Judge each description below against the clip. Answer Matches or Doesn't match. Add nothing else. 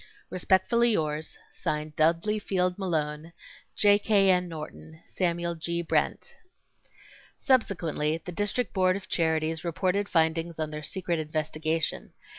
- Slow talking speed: Matches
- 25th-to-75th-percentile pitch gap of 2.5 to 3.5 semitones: Matches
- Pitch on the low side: Doesn't match